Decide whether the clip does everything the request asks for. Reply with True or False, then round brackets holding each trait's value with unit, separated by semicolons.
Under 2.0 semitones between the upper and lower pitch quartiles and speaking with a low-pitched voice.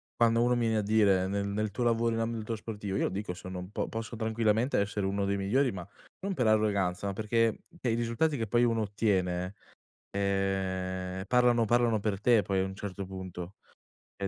False (2.9 semitones; 105 Hz)